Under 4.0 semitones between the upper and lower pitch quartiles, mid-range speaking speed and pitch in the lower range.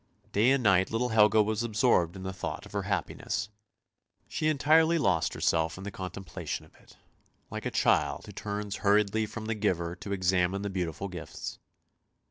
Yes: average, 3.2 semitones; average, 175 wpm; low, 100 Hz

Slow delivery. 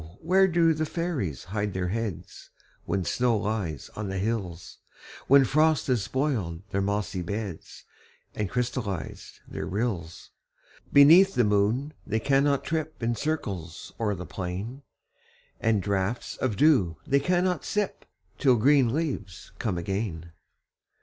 Yes: slow, 130 wpm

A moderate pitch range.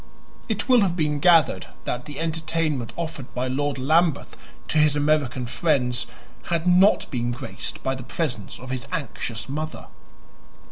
Yes: average, 4.4 semitones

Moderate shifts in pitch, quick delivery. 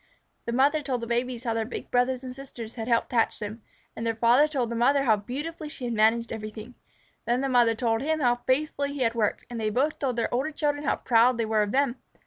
Yes: average, 3.1 semitones; fast, 245 wpm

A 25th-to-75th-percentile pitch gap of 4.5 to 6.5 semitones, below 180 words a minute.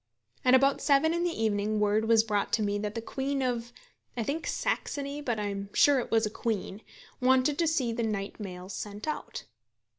No: average, 4.8 semitones; fast, 205 wpm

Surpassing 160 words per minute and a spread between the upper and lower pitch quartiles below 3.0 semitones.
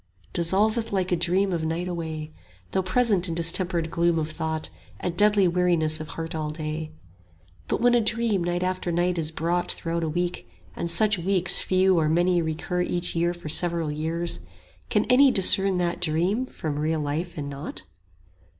Yes: average, 180 wpm; narrow, 2.5 semitones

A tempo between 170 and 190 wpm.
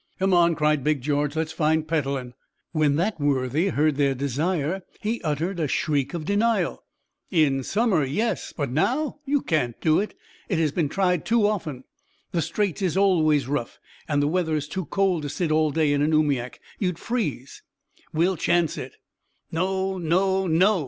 Yes: average, 175 wpm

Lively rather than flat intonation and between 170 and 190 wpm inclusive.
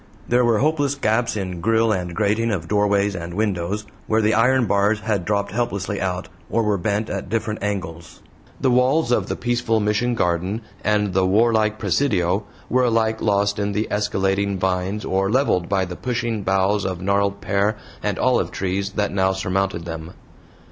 No: average, 2.7 semitones; average, 175 wpm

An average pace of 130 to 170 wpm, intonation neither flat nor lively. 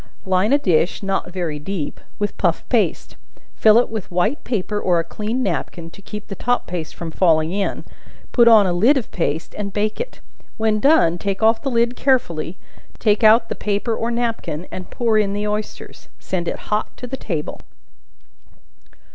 No: average, 180 wpm; average, 4.3 semitones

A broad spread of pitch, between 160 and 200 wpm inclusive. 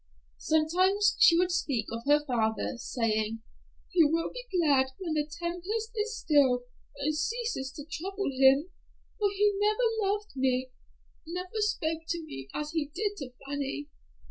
No: wide, 6.4 semitones; average, 150 wpm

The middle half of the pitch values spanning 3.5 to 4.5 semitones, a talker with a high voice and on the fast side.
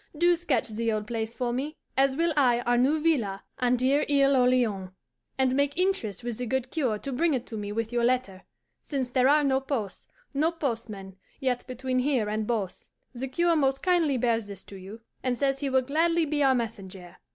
Yes: average, 3.8 semitones; very high, 255 Hz; fast, 210 wpm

